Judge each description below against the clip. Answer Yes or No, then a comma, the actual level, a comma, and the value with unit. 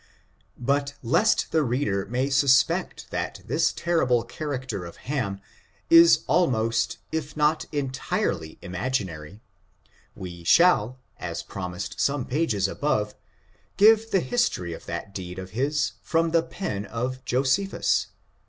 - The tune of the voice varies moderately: No, wide, 7.1 semitones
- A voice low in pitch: Yes, low, 130 Hz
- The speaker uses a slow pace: Yes, slow, 125 wpm